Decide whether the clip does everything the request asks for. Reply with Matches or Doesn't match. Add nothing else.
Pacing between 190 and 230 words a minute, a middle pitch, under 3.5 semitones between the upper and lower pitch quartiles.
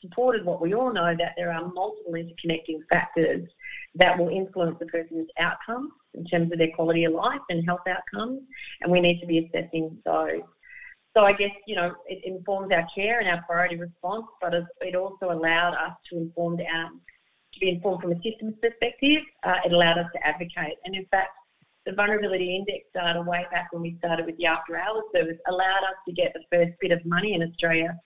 Matches